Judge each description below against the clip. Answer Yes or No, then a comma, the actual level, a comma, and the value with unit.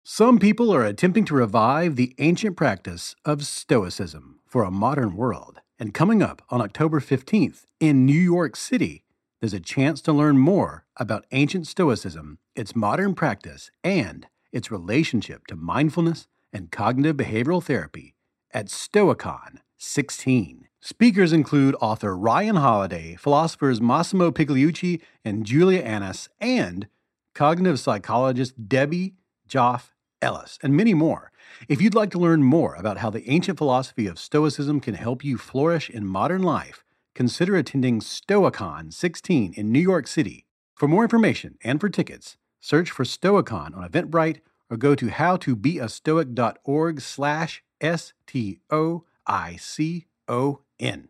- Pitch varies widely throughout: Yes, wide, 6.3 semitones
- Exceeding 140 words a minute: No, slow, 135 wpm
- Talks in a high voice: No, medium, 140 Hz